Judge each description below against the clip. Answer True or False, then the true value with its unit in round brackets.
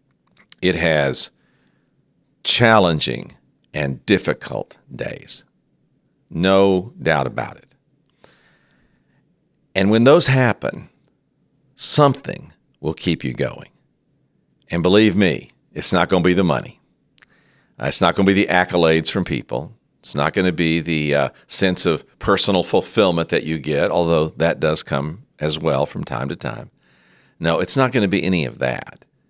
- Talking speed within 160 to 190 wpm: False (145 wpm)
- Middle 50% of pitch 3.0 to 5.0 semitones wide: False (5.5 semitones)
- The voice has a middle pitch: False (85 Hz)